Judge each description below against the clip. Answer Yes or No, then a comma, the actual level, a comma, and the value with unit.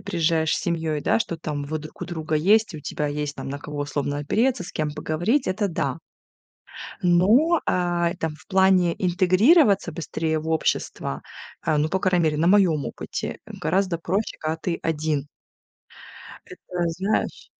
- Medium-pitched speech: Yes, medium, 170 Hz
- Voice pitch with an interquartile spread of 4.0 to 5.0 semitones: No, average, 3.4 semitones